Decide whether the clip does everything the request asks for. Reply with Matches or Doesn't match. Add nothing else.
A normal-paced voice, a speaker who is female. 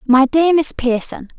Matches